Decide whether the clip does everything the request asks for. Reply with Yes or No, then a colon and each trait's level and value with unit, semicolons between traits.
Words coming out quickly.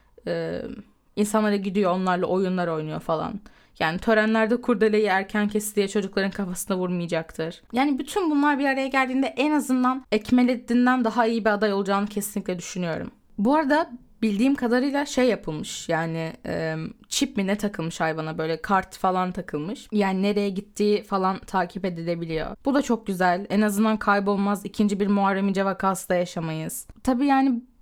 Yes: fast, 150 wpm